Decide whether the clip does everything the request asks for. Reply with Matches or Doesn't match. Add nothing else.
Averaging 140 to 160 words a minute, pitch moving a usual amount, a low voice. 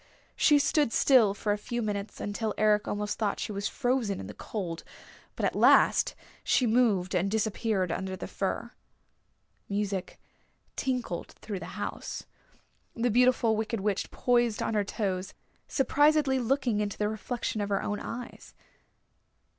Doesn't match